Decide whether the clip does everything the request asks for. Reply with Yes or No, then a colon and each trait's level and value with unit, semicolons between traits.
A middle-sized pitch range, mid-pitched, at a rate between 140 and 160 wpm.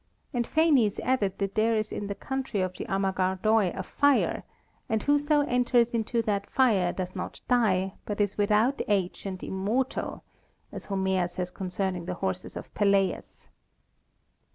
No: average, 4.0 semitones; high, 205 Hz; average, 155 wpm